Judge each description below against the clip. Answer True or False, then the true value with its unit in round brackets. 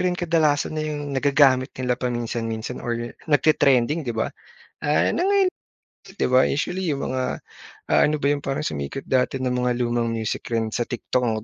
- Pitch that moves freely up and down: False (3.8 semitones)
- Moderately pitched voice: False (130 Hz)